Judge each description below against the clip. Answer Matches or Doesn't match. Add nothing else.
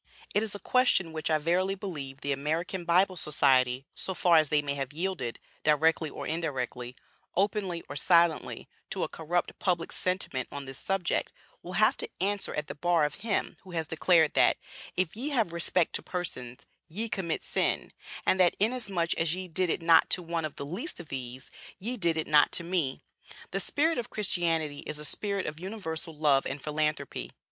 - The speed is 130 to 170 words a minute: Doesn't match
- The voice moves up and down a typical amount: Matches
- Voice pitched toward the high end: Doesn't match